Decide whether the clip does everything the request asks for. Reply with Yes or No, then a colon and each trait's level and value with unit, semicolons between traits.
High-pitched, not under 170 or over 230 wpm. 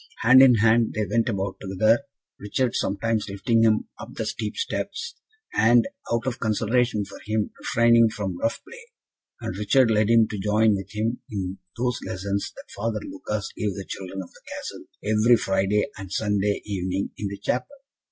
No: low, 105 Hz; average, 175 wpm